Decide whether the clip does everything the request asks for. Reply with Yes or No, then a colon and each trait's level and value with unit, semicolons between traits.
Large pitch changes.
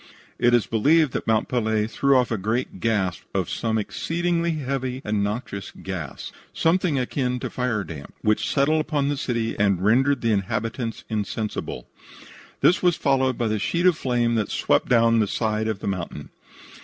No: average, 4.3 semitones